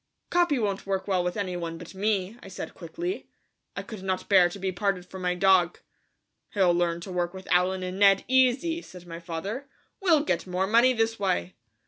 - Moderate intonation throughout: Yes, average, 3.4 semitones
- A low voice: No, high, 190 Hz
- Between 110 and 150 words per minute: No, average, 200 wpm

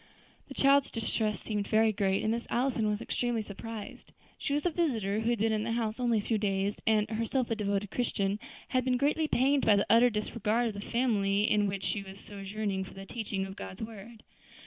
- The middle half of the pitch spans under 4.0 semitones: Yes, average, 2.8 semitones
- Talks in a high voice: Yes, high, 220 Hz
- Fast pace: Yes, fast, 215 wpm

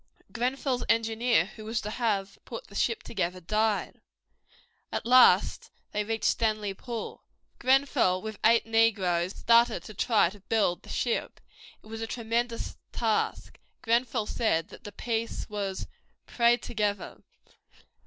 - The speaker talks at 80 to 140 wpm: Yes, slow, 135 wpm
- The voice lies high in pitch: Yes, high, 225 Hz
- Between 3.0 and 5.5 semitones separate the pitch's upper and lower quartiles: No, narrow, 2.4 semitones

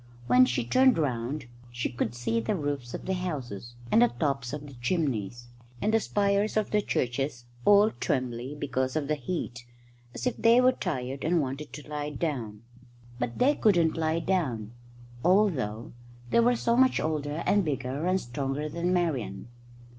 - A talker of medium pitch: Yes, medium, 145 Hz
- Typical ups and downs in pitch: No, wide, 6.8 semitones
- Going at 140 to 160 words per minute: No, average, 170 wpm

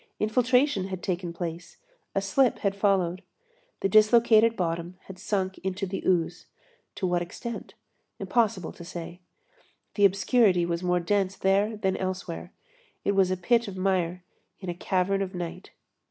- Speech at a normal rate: Yes, average, 155 wpm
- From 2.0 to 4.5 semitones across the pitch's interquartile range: Yes, narrow, 2.4 semitones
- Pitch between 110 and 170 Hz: No, high, 190 Hz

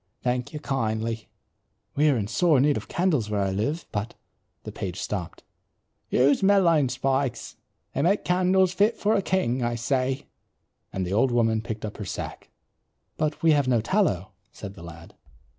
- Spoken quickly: No, average, 175 wpm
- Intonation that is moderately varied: No, wide, 6.6 semitones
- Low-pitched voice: Yes, low, 130 Hz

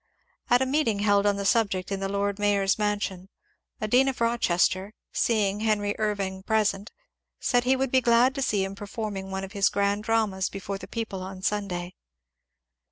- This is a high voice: Yes, high, 205 Hz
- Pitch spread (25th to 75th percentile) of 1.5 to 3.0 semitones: Yes, narrow, 2.6 semitones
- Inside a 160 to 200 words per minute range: Yes, average, 180 wpm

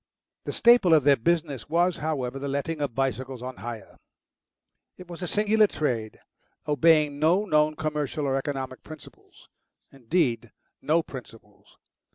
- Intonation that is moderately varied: Yes, average, 3.9 semitones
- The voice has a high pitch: No, medium, 145 Hz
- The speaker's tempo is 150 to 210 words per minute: No, average, 140 wpm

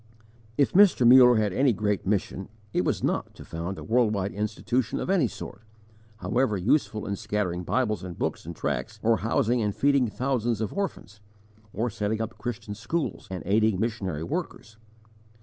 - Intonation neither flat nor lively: Yes, average, 3.3 semitones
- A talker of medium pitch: No, low, 110 Hz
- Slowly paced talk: No, average, 170 wpm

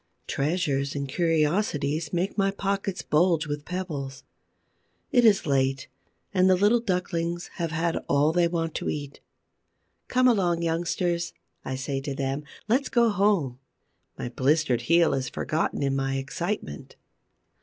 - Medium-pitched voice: Yes, medium, 165 Hz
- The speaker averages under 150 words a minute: Yes, average, 140 wpm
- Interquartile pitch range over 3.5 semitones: Yes, average, 4.8 semitones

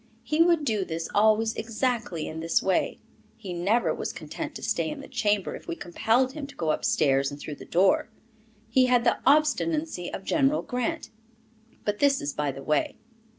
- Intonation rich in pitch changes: Yes, wide, 7.8 semitones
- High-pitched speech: Yes, high, 220 Hz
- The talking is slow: No, average, 190 wpm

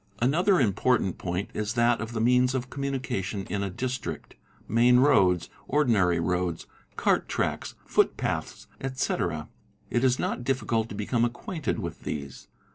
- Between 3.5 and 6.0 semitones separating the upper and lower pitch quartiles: Yes, average, 4.9 semitones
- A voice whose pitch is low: Yes, low, 120 Hz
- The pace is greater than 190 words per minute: No, average, 140 wpm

